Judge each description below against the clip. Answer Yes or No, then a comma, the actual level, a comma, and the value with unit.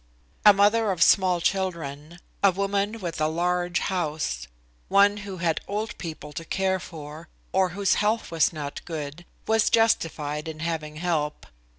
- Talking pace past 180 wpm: No, average, 155 wpm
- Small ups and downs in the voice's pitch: No, average, 4.2 semitones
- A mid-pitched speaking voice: Yes, medium, 175 Hz